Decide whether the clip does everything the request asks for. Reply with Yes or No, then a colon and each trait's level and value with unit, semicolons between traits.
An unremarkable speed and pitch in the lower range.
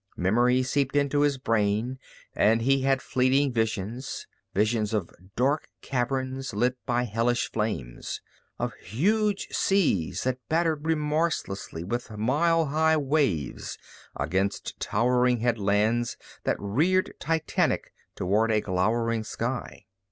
No: slow, 115 wpm; low, 125 Hz